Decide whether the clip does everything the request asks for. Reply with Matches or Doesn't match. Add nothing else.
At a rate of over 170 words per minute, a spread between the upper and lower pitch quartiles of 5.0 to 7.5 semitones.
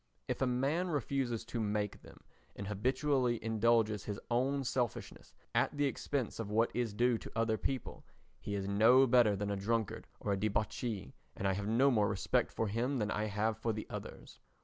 Doesn't match